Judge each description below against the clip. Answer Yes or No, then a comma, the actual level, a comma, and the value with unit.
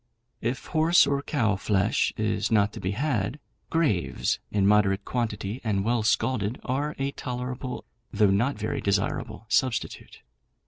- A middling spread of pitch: Yes, average, 4.3 semitones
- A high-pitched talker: No, low, 115 Hz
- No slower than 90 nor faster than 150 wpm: Yes, average, 140 wpm